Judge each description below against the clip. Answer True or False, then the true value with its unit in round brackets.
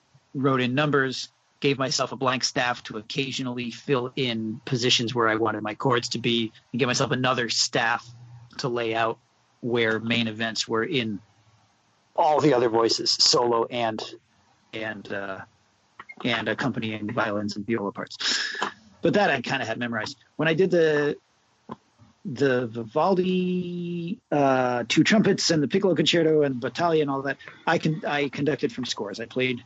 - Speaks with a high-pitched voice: False (125 Hz)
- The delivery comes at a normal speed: True (165 wpm)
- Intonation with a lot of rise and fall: False (3.9 semitones)